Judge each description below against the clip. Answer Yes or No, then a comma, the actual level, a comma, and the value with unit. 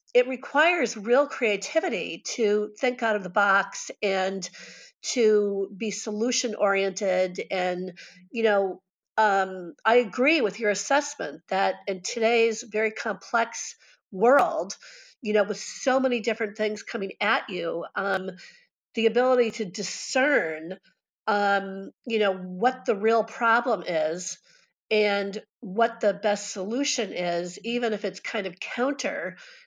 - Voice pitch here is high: Yes, high, 215 Hz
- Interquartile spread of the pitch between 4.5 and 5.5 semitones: No, average, 3.6 semitones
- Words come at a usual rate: No, slow, 130 wpm